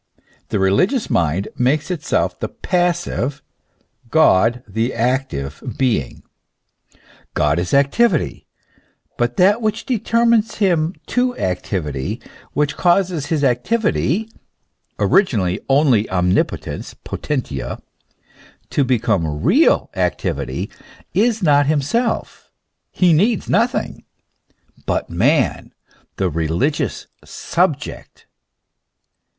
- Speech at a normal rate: No, slow, 90 wpm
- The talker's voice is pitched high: No, medium, 140 Hz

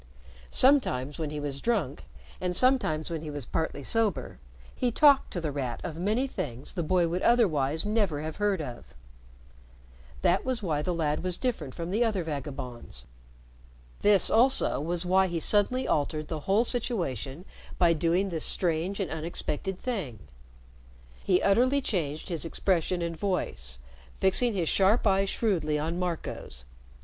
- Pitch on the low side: No, medium, 175 Hz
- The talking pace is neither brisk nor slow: Yes, average, 155 wpm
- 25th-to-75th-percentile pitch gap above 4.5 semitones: Yes, average, 5.2 semitones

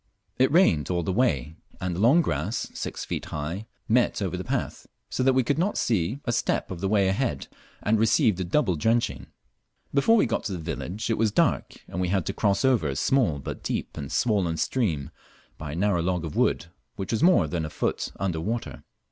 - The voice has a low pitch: Yes, very low, 95 Hz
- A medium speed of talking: No, fast, 215 wpm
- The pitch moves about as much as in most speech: No, wide, 6.3 semitones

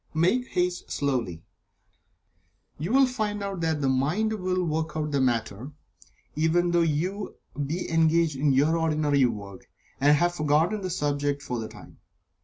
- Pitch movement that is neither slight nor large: Yes, average, 3.9 semitones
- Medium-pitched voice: Yes, medium, 155 Hz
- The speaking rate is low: No, average, 150 wpm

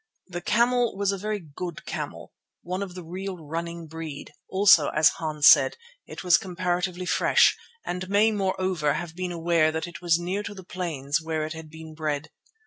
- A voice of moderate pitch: Yes, medium, 175 Hz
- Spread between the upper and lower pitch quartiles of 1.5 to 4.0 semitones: Yes, average, 2.9 semitones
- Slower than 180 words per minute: No, average, 185 wpm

